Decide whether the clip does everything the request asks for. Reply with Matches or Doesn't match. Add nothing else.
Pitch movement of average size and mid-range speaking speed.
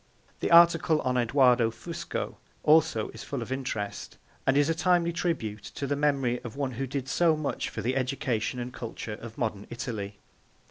Matches